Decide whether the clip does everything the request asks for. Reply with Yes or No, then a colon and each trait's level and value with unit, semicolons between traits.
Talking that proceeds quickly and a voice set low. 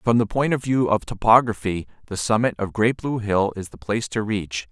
Yes: fast, 230 wpm; low, 110 Hz